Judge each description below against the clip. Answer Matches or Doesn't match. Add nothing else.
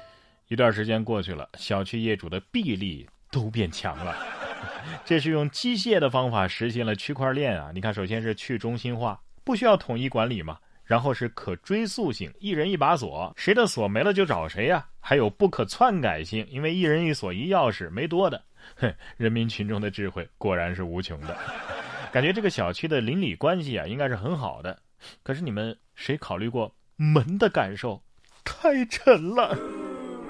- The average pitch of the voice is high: Doesn't match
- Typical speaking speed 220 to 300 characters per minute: Matches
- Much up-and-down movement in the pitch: Matches